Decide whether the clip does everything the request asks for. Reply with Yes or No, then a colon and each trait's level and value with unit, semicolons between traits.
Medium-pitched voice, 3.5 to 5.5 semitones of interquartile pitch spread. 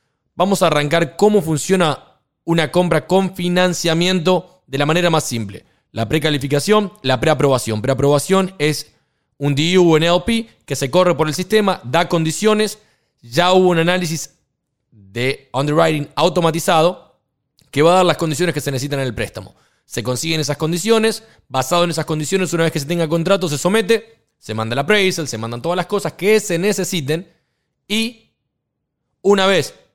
Yes: medium, 165 Hz; average, 4.5 semitones